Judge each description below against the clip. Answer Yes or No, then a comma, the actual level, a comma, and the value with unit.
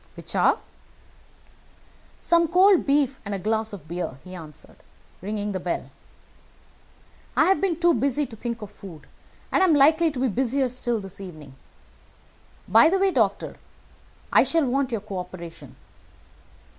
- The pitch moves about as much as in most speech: No, wide, 7.6 semitones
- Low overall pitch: No, high, 235 Hz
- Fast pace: No, average, 155 wpm